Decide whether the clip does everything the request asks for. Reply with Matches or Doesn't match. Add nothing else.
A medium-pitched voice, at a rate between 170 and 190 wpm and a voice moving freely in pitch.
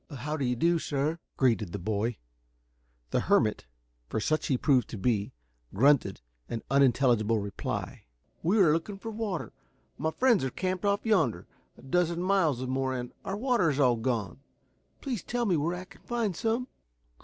Matches